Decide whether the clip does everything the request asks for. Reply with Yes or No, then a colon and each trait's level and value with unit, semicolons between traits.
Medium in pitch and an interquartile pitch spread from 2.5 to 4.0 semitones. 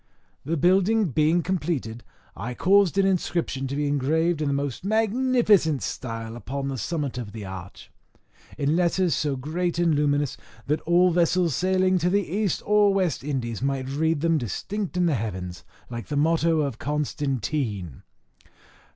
No: medium, 155 Hz; average, 5.1 semitones